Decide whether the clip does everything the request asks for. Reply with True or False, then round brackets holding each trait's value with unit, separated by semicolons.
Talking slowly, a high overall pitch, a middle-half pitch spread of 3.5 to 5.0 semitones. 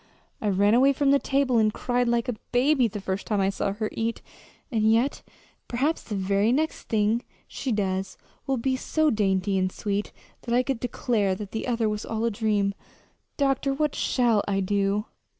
False (185 wpm; 225 Hz; 3.9 semitones)